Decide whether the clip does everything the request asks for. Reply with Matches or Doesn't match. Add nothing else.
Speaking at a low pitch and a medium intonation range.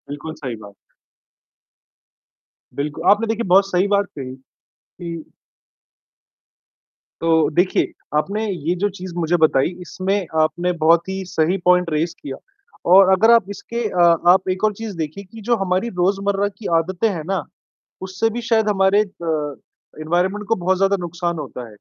Doesn't match